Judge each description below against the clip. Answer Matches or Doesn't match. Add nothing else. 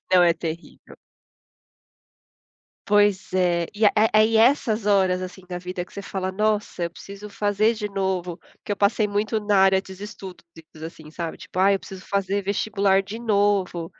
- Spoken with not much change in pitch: Matches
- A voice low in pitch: Doesn't match